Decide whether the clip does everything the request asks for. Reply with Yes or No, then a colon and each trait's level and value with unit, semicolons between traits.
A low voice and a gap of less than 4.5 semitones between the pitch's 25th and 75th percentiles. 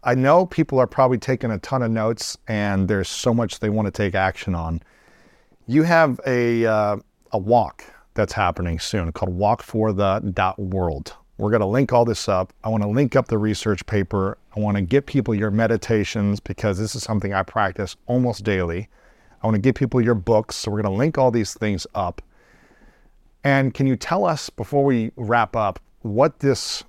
Yes: low, 110 Hz; average, 3.8 semitones